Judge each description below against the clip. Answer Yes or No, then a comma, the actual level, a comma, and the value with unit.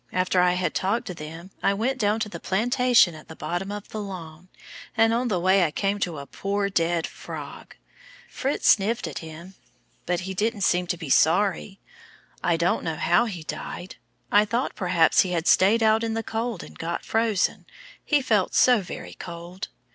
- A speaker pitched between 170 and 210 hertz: Yes, high, 190 Hz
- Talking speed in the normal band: Yes, average, 195 wpm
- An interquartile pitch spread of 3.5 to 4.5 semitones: Yes, average, 4.1 semitones